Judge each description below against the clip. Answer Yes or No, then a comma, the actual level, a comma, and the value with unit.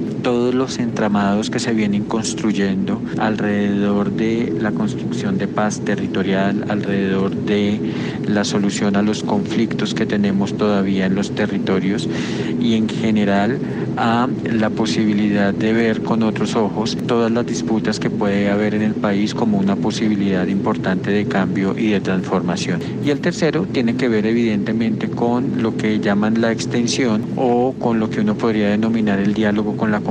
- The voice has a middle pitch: No, low, 105 Hz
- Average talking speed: Yes, average, 160 wpm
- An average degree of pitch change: No, narrow, 2.1 semitones